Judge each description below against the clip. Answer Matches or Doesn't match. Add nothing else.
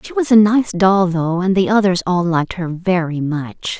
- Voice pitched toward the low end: Doesn't match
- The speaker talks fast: Matches